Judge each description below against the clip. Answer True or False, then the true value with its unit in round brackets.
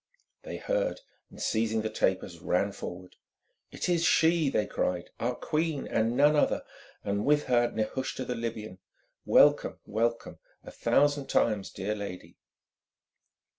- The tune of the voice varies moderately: False (6.1 semitones)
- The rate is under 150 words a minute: True (135 wpm)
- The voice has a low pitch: True (115 Hz)